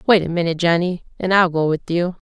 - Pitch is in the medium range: Yes, medium, 175 Hz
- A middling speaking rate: No, fast, 240 wpm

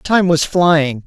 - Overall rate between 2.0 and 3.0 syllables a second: Yes, 2.9 syllables/s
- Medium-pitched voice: Yes, medium, 165 Hz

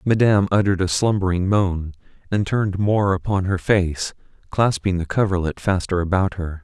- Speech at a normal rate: Yes, average, 155 wpm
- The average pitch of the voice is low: Yes, very low, 95 Hz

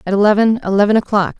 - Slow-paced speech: Yes, slow, 130 wpm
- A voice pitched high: Yes, high, 205 Hz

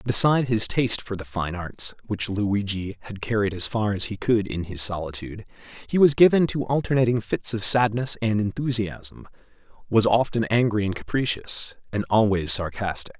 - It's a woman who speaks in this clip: No, male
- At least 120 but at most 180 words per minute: Yes, average, 170 wpm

